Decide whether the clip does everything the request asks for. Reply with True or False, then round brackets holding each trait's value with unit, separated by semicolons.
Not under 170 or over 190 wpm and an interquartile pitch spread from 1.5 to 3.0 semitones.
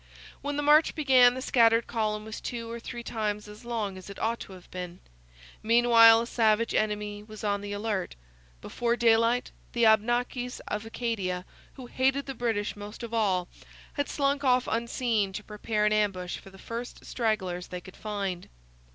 True (175 wpm; 2.7 semitones)